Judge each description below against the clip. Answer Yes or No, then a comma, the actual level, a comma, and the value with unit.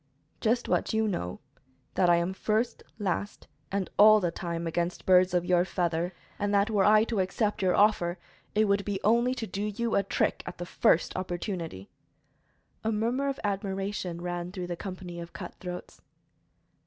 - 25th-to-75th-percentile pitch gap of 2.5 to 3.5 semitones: Yes, average, 3.2 semitones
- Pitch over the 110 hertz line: Yes, high, 190 Hz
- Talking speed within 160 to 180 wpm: Yes, average, 175 wpm